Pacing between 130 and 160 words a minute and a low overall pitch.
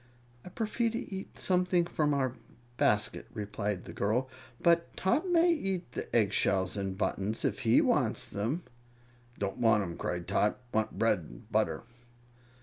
Yes: average, 155 wpm; low, 115 Hz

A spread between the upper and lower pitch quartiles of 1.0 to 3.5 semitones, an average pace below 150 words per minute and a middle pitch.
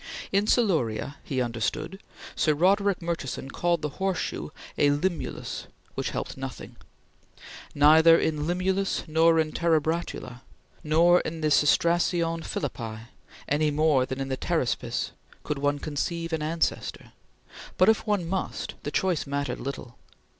Yes: average, 3.2 semitones; average, 140 wpm; medium, 160 Hz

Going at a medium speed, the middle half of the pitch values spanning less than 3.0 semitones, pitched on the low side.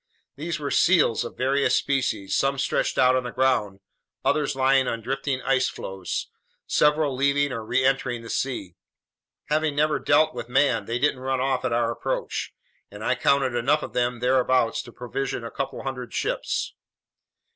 Yes: average, 165 wpm; narrow, 2.4 semitones; low, 130 Hz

